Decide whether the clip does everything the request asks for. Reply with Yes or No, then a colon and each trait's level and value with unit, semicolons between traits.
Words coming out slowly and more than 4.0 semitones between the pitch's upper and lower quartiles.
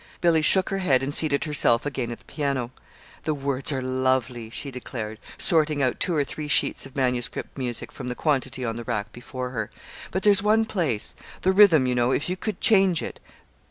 No: fast, 205 wpm; average, 4.6 semitones